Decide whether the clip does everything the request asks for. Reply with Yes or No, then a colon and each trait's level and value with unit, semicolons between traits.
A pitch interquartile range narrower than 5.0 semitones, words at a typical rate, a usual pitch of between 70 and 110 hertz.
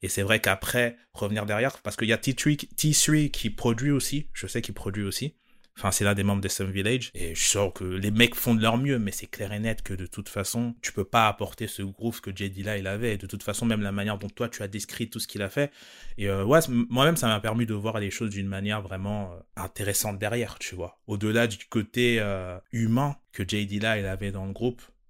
No: average, 3.1 semitones; fast, 250 wpm; low, 105 Hz